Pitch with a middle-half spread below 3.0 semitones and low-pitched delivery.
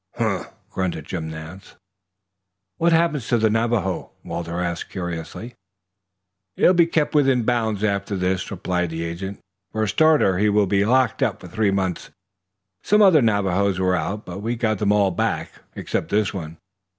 No: average, 4.2 semitones; low, 100 Hz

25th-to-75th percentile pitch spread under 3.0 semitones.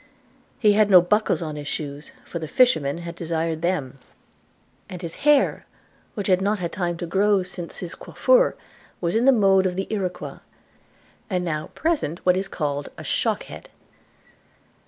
No: average, 3.7 semitones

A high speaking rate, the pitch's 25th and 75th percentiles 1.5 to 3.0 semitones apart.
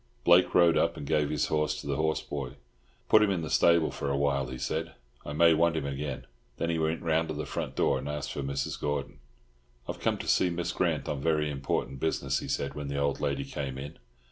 Yes: fast, 245 wpm; narrow, 2.6 semitones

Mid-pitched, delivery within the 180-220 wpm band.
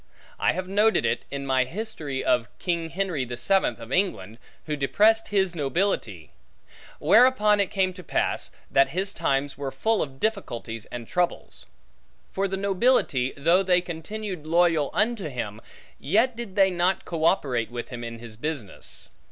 No: medium, 170 Hz; average, 160 wpm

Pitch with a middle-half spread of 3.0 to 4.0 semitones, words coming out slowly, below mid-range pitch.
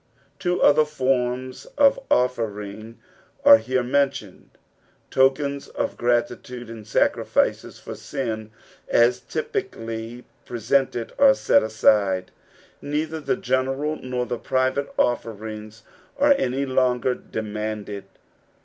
Yes: average, 3.6 semitones; slow, 115 wpm; low, 125 Hz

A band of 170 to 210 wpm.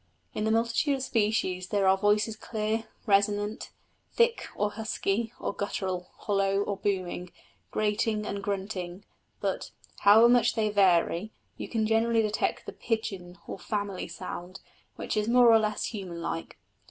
No: average, 150 wpm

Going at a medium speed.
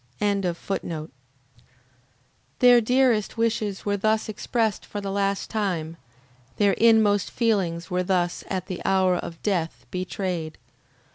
No: slow, 120 wpm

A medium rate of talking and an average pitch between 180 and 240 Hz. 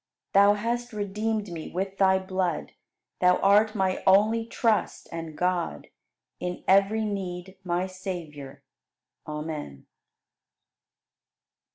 No: slow, 100 wpm; high, 190 Hz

